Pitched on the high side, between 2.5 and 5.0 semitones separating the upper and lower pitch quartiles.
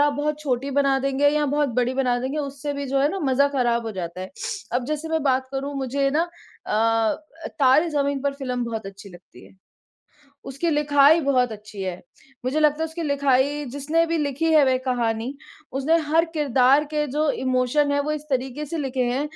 Yes: very high, 275 Hz; average, 2.8 semitones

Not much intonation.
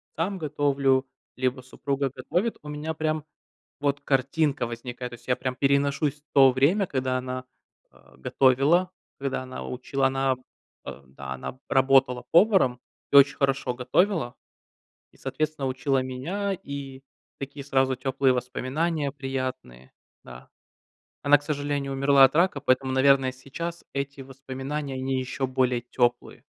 Yes: narrow, 1.9 semitones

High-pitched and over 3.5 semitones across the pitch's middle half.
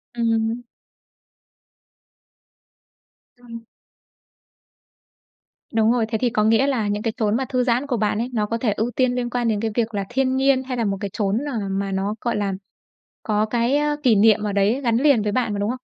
No: high, 230 Hz; average, 2.9 semitones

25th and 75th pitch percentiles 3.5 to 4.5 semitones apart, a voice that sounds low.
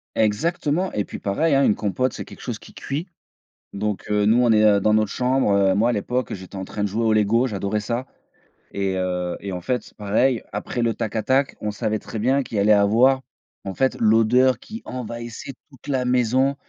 Yes: average, 3.8 semitones; low, 110 Hz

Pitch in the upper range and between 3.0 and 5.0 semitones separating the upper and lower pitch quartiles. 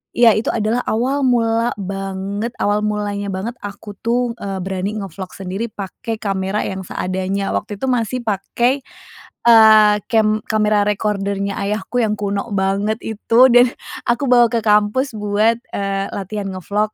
No: high, 210 Hz; narrow, 2.5 semitones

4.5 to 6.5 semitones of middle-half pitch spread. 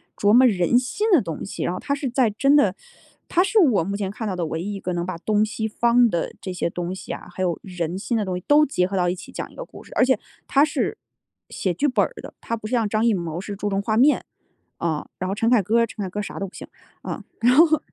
Yes: average, 5.2 semitones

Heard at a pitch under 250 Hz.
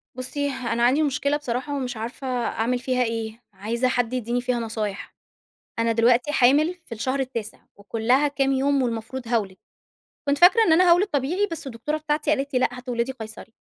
No: very high, 255 Hz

